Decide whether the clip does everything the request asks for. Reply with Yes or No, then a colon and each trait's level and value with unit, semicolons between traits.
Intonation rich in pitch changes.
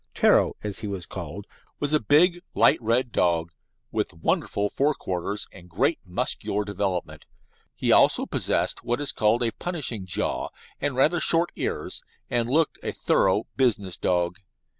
Yes: wide, 6.7 semitones